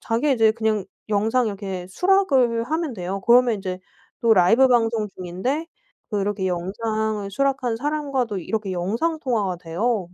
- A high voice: Yes, high, 220 Hz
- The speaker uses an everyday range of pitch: Yes, average, 4.6 semitones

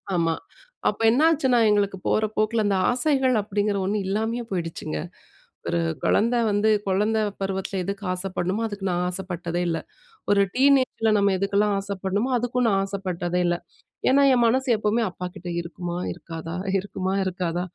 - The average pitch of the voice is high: Yes, high, 200 Hz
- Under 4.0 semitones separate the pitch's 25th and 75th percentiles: Yes, average, 3.5 semitones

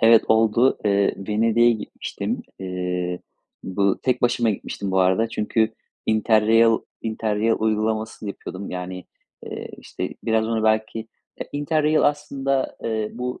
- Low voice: Yes, low, 110 Hz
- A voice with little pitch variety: Yes, narrow, 2.3 semitones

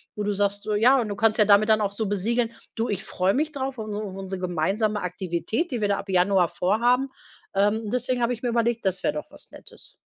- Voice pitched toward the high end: Yes, high, 210 Hz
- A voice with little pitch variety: No, average, 3.2 semitones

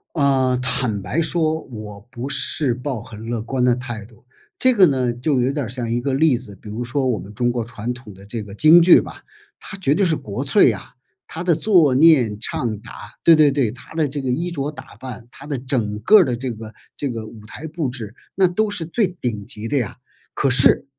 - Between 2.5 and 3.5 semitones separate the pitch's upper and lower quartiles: No, average, 5.0 semitones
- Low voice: Yes, low, 130 Hz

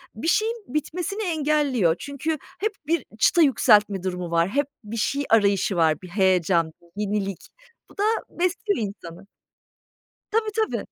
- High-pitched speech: Yes, high, 220 Hz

